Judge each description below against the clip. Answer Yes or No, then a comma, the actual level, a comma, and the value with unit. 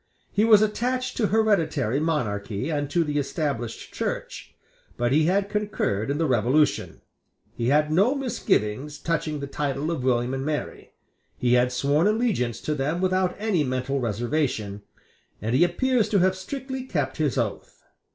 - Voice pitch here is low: No, medium, 150 Hz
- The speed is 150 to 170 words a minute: Yes, average, 160 wpm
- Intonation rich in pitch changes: Yes, wide, 7.2 semitones